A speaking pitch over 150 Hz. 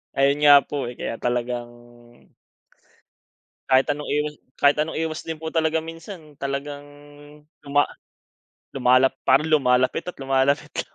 No: medium, 145 Hz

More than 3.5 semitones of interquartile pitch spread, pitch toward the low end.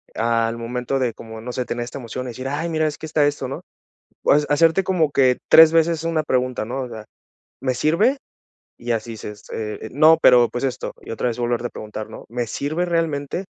Yes: average, 4.8 semitones; low, 130 Hz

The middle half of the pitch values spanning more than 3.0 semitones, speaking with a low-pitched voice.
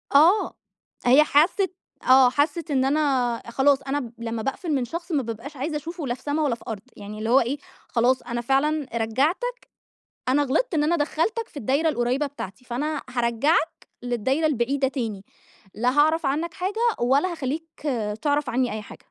No: average, 4.2 semitones; very high, 275 Hz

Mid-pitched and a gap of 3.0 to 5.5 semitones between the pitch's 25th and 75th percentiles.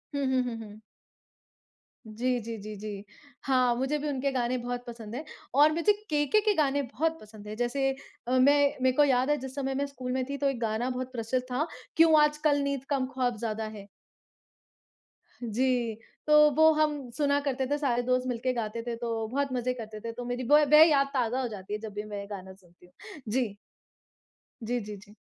No: very high, 255 Hz; average, 3.7 semitones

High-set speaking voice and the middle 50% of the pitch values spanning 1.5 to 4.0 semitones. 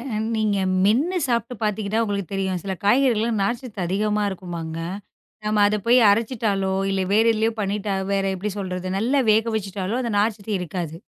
Yes: high, 210 Hz; narrow, 2.6 semitones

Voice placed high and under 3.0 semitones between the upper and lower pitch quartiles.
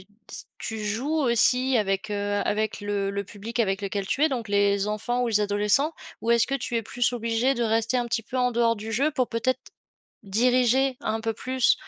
No: high, 230 Hz; average, 3.3 semitones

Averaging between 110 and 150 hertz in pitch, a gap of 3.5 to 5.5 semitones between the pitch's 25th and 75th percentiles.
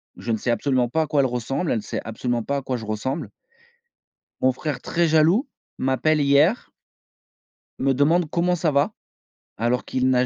Yes: low, 135 Hz; average, 4.0 semitones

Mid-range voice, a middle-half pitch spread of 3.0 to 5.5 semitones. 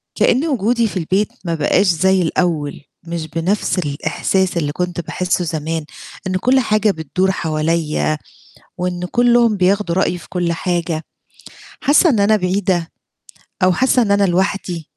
Yes: medium, 180 Hz; average, 3.4 semitones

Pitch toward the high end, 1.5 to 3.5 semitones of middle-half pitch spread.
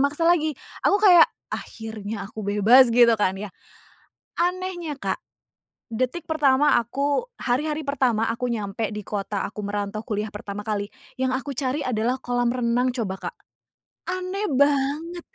No: very high, 250 Hz; wide, 5.6 semitones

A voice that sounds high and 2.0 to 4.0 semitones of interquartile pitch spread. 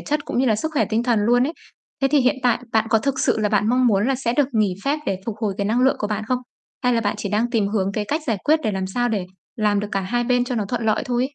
Yes: high, 230 Hz; average, 3.3 semitones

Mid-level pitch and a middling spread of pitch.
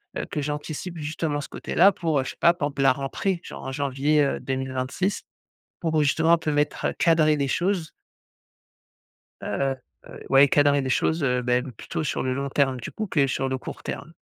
Yes: medium, 145 Hz; average, 3.1 semitones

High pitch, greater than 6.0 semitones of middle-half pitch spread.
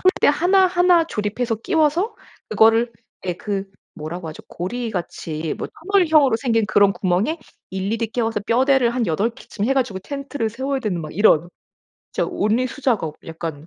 Yes: high, 225 Hz; wide, 6.4 semitones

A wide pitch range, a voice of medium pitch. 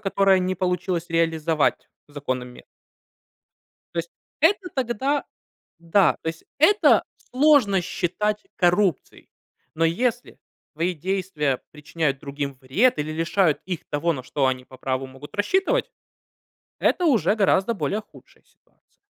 Yes: wide, 5.8 semitones; medium, 175 Hz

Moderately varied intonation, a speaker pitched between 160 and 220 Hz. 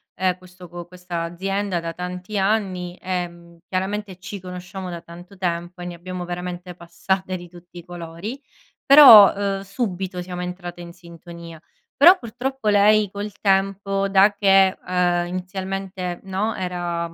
No: narrow, 1.9 semitones; medium, 185 Hz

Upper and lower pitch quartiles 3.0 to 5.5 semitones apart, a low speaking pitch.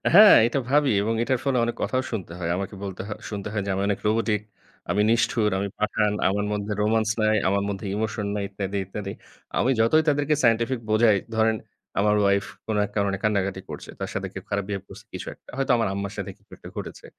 No: narrow, 2.4 semitones; low, 105 Hz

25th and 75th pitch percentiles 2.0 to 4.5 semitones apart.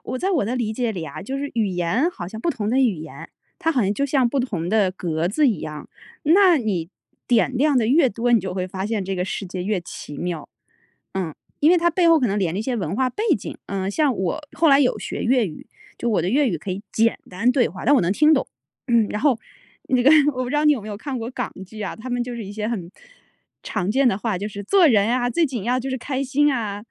No: wide, 5.5 semitones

